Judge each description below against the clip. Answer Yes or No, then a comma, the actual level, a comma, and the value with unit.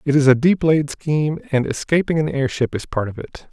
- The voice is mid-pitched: Yes, medium, 145 Hz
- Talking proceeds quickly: Yes, fast, 255 wpm